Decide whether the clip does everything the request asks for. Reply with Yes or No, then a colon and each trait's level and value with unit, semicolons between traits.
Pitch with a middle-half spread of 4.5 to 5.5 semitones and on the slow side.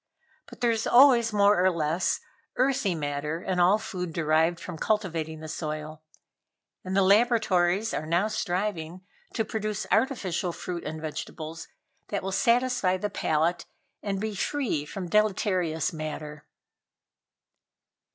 Yes: average, 4.9 semitones; slow, 130 wpm